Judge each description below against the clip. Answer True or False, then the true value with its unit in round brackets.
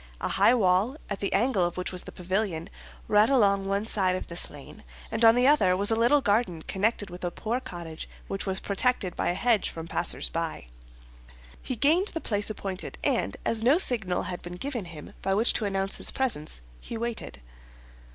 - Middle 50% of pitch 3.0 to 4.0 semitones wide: False (4.5 semitones)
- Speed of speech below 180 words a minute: False (200 wpm)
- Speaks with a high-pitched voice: True (200 Hz)